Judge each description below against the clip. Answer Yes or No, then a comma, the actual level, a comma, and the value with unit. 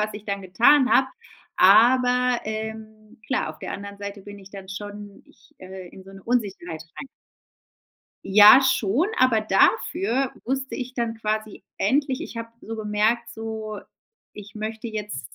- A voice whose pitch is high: Yes, high, 215 Hz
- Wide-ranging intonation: No, average, 2.9 semitones